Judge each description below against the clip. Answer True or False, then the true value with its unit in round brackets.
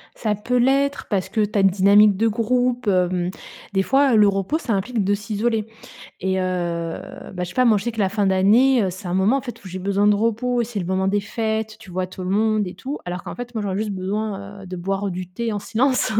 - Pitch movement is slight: False (3.3 semitones)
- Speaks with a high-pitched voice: True (205 Hz)